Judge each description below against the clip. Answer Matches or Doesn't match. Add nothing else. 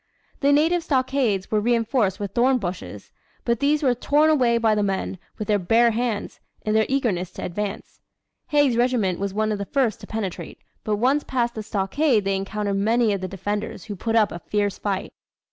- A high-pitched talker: Matches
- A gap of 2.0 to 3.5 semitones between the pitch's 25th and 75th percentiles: Doesn't match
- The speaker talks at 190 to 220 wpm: Matches